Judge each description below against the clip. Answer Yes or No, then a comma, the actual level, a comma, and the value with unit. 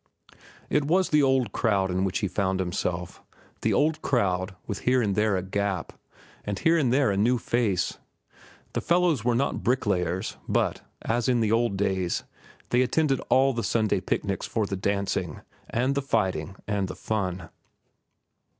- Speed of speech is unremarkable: Yes, average, 160 wpm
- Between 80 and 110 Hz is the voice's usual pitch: Yes, low, 105 Hz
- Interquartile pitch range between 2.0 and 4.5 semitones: No, average, 5.0 semitones